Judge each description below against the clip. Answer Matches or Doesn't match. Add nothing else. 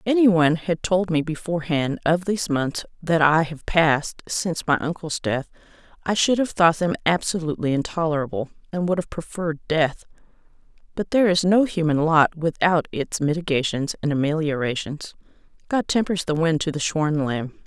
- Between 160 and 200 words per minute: Matches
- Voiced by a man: Doesn't match